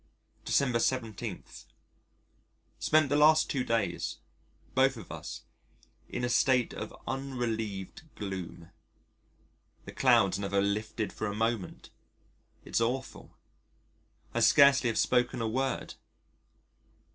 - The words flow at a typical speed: No, slow, 110 wpm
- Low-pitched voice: Yes, low, 120 Hz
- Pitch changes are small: No, average, 3.7 semitones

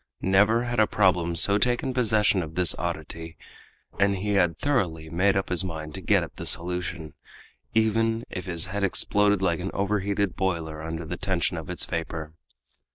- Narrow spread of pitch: No, average, 3.7 semitones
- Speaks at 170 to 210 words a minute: Yes, average, 175 wpm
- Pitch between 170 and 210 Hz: No, very low, 95 Hz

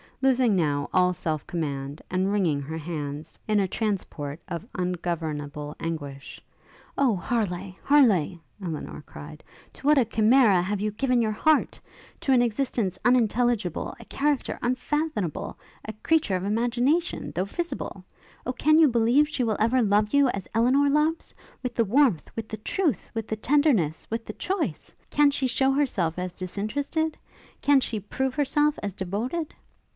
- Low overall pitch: No, high, 220 Hz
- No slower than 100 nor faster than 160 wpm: Yes, average, 155 wpm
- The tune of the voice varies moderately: No, wide, 6.9 semitones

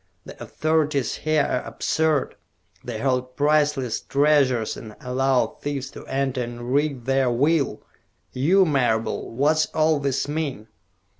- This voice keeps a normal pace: No, slow, 130 wpm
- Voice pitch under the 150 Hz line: Yes, medium, 140 Hz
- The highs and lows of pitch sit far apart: No, average, 3.2 semitones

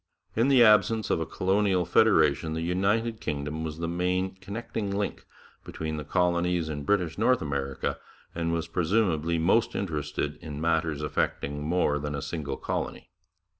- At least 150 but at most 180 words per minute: Yes, average, 155 wpm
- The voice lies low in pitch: Yes, very low, 85 Hz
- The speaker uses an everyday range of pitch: Yes, average, 4.4 semitones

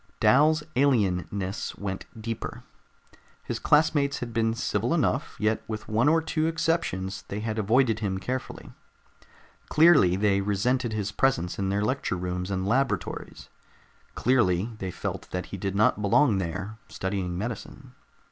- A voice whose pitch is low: Yes, low, 110 Hz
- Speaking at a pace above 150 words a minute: No, average, 140 wpm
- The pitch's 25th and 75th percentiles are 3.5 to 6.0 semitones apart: Yes, average, 5.1 semitones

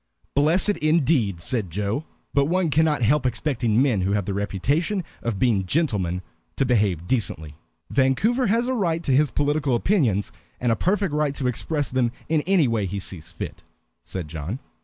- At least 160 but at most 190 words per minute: Yes, average, 175 wpm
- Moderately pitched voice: No, low, 130 Hz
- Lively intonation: Yes, wide, 7.4 semitones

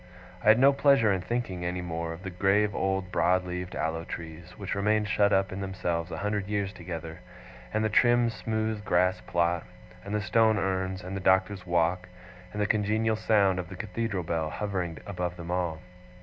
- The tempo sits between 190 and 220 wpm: Yes, average, 195 wpm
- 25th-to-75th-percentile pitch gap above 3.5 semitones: No, average, 3.0 semitones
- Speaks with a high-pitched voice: No, very low, 95 Hz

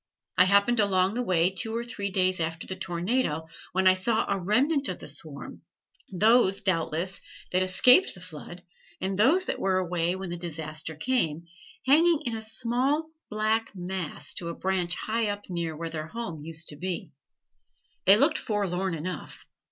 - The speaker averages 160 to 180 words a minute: Yes, average, 175 wpm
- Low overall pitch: No, high, 190 Hz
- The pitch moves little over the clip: No, average, 4.4 semitones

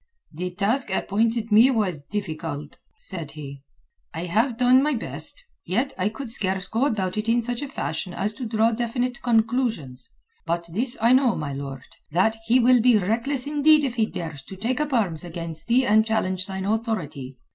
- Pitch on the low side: No, high, 220 Hz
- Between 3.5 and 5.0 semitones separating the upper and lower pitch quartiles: No, wide, 5.6 semitones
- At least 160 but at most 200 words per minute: Yes, average, 185 wpm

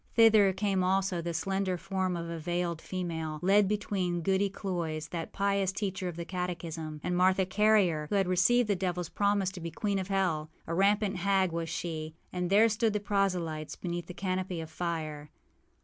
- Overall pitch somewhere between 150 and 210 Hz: Yes, medium, 185 Hz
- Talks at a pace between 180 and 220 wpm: Yes, average, 185 wpm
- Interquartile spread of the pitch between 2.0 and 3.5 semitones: Yes, average, 2.7 semitones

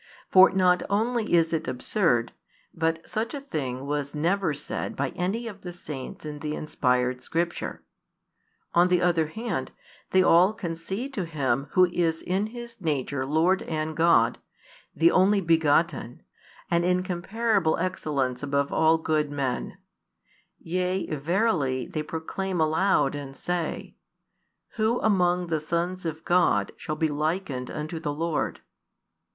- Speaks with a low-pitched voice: No, medium, 165 Hz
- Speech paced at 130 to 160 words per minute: Yes, average, 140 wpm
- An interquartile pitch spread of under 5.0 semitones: Yes, average, 3.7 semitones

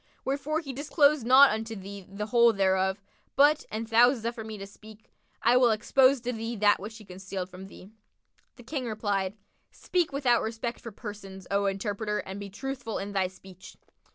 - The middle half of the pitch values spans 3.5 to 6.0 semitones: Yes, average, 3.8 semitones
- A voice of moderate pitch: No, high, 220 Hz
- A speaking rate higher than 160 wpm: Yes, average, 180 wpm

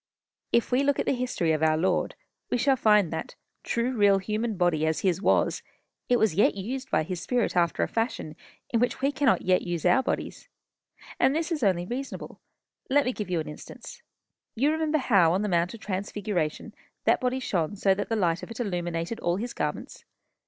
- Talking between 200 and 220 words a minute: Yes, fast, 205 wpm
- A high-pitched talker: Yes, high, 205 Hz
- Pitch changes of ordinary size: No, wide, 6.1 semitones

